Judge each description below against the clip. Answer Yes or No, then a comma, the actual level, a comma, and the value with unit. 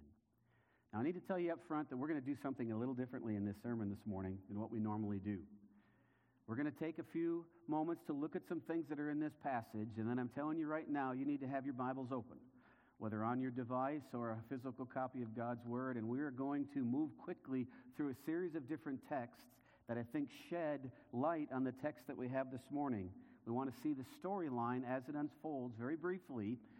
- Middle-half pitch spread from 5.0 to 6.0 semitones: No, average, 4.3 semitones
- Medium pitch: No, low, 130 Hz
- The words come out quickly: Yes, fast, 235 wpm